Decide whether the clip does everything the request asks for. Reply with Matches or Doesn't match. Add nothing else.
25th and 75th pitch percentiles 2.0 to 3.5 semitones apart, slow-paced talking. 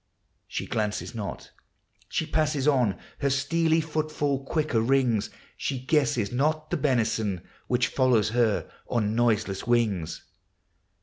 Doesn't match